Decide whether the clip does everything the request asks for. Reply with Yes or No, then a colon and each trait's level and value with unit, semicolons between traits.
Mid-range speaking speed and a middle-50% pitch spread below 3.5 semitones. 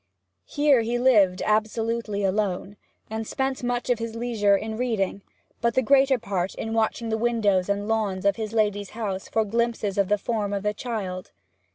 Yes: average, 180 wpm; average, 2.7 semitones